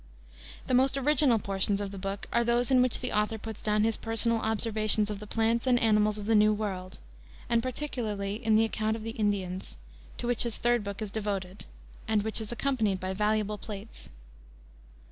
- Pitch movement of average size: No, narrow, 2.1 semitones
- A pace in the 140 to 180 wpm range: No, average, 190 wpm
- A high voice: Yes, high, 215 Hz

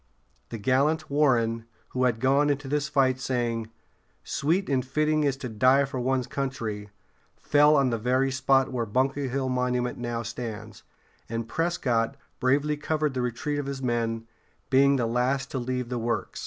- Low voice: Yes, low, 130 Hz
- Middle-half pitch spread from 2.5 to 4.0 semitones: Yes, average, 2.8 semitones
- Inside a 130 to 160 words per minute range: No, average, 170 wpm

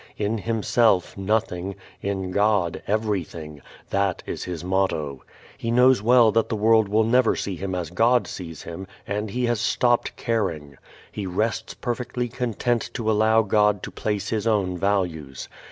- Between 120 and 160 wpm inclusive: Yes, average, 155 wpm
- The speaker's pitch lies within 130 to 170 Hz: No, low, 105 Hz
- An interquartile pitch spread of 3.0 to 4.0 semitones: Yes, average, 3.7 semitones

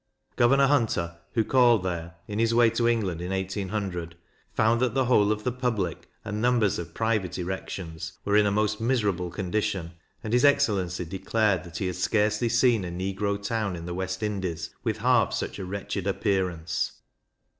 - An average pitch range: Yes, average, 3.8 semitones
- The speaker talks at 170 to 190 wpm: Yes, average, 175 wpm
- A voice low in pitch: Yes, low, 100 Hz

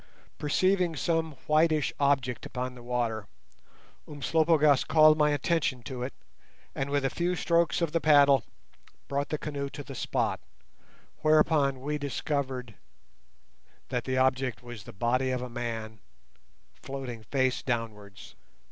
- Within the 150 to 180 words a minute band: No, slow, 135 wpm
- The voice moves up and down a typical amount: Yes, average, 3.6 semitones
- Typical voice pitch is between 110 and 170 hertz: Yes, medium, 140 Hz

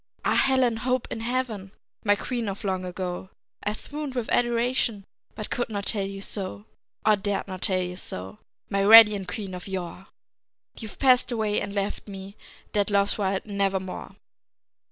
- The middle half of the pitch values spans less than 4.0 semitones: Yes, average, 3.0 semitones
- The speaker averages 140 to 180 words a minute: Yes, average, 170 wpm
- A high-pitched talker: Yes, high, 205 Hz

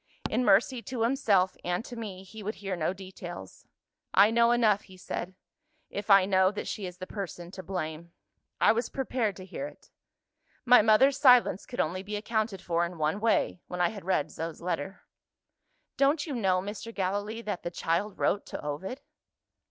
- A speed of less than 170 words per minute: No, average, 185 wpm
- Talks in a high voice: Yes, high, 195 Hz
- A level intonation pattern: No, average, 3.8 semitones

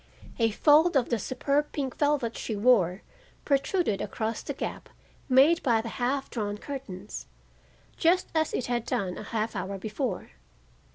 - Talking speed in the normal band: Yes, average, 155 wpm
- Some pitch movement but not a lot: Yes, average, 4.9 semitones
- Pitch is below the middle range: No, high, 245 Hz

